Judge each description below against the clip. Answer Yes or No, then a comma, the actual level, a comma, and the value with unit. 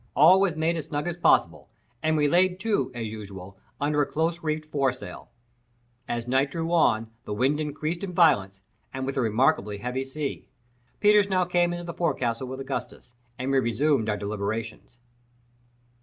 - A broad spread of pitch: Yes, wide, 6.1 semitones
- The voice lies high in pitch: No, medium, 140 Hz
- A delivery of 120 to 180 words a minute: Yes, average, 170 wpm